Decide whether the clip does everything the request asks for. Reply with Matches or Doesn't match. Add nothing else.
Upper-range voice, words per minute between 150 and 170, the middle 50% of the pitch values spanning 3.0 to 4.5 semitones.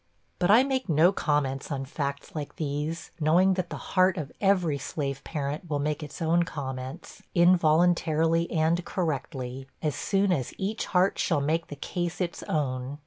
Doesn't match